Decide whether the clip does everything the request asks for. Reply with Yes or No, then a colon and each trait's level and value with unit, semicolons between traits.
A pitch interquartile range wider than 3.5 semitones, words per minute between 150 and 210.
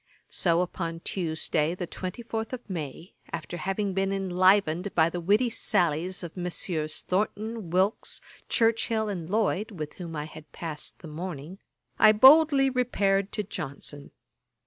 No: average, 4.2 semitones; average, 140 wpm